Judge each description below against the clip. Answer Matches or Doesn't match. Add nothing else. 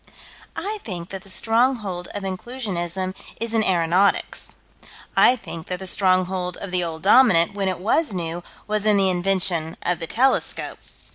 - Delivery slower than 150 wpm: Doesn't match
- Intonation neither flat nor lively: Matches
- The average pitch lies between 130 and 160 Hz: Doesn't match